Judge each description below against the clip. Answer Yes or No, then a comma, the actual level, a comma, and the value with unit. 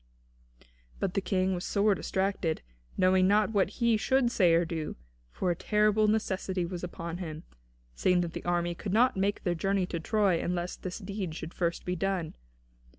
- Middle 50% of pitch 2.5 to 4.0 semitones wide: Yes, average, 2.8 semitones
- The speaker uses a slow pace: No, average, 180 wpm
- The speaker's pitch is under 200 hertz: Yes, medium, 185 Hz